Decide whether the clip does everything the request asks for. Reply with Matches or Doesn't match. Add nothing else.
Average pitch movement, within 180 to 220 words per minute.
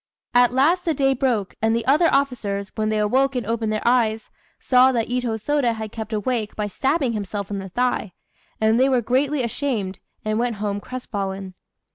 Matches